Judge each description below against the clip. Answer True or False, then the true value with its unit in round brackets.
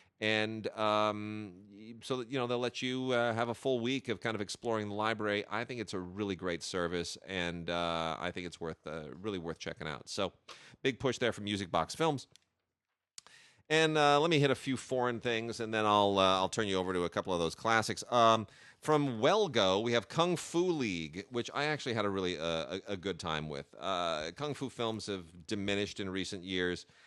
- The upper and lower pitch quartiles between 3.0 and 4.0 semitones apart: False (4.6 semitones)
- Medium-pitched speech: False (110 Hz)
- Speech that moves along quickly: True (215 wpm)